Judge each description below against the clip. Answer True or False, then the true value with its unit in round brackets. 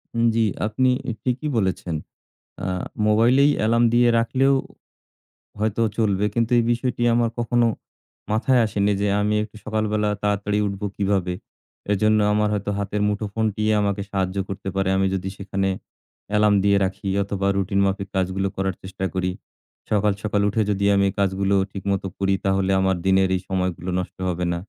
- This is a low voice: True (100 Hz)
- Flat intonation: True (2.1 semitones)